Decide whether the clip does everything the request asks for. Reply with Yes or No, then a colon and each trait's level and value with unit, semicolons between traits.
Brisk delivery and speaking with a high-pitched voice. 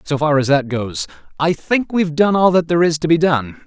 No: fast, 280 wpm; medium, 155 Hz